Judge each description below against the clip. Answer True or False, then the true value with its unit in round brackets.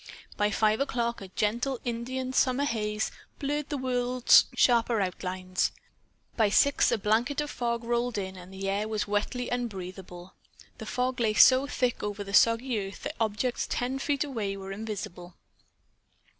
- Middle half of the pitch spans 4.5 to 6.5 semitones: False (3.9 semitones)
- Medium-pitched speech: False (230 Hz)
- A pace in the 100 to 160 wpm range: True (155 wpm)